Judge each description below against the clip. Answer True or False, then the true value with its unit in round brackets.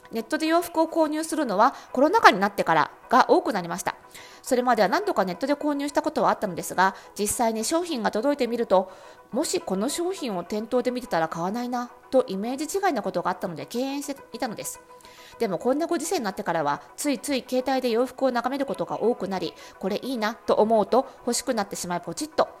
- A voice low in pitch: False (250 Hz)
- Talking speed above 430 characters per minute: True (450 characters per minute)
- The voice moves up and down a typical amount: False (6.2 semitones)